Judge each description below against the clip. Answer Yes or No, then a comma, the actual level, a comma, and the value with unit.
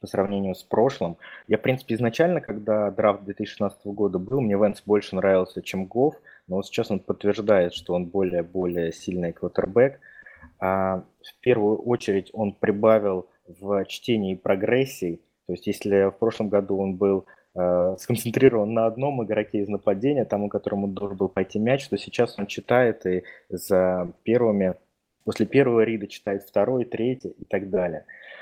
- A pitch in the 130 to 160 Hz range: No, low, 100 Hz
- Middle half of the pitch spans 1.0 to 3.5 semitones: Yes, average, 2.9 semitones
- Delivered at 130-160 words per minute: Yes, average, 155 wpm